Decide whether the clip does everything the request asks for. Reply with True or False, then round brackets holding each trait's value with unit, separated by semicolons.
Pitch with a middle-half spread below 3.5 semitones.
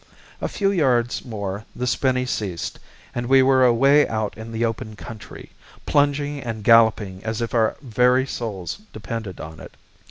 True (3.1 semitones)